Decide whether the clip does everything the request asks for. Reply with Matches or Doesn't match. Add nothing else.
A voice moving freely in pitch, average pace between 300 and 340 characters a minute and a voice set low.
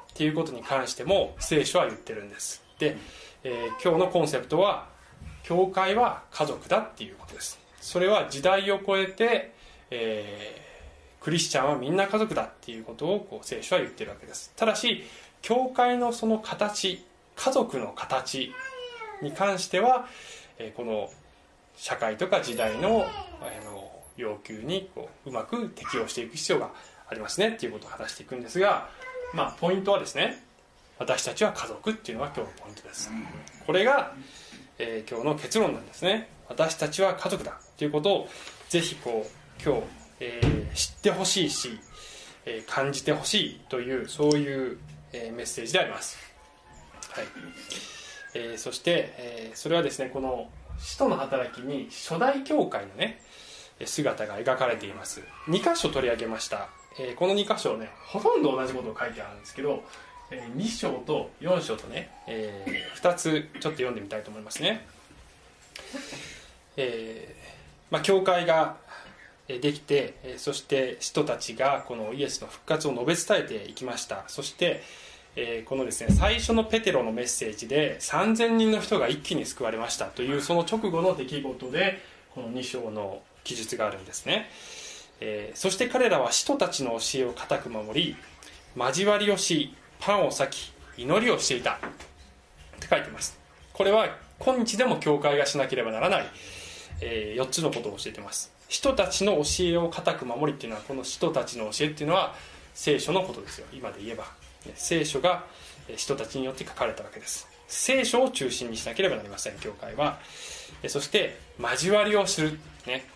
Doesn't match